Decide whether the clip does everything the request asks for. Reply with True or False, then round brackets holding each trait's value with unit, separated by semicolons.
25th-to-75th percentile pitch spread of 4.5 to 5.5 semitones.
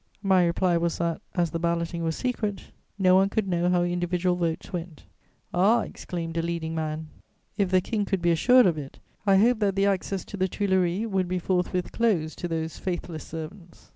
False (2.5 semitones)